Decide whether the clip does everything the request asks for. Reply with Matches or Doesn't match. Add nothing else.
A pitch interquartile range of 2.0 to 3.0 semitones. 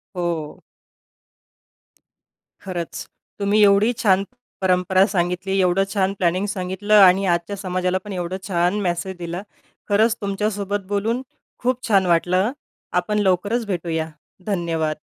Matches